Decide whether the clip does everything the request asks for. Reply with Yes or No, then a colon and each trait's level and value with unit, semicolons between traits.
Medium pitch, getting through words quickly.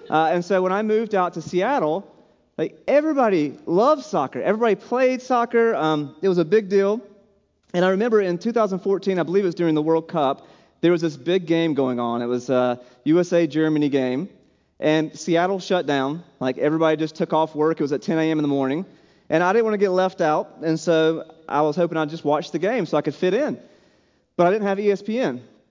Yes: medium, 170 Hz; fast, 220 wpm